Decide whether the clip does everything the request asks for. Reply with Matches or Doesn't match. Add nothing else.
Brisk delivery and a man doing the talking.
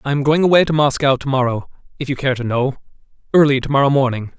Matches